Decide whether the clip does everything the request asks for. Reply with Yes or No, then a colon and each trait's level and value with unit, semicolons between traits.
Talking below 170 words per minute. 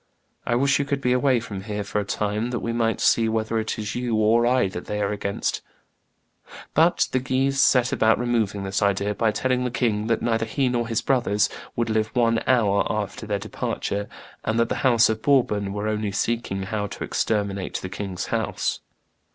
No: average, 200 wpm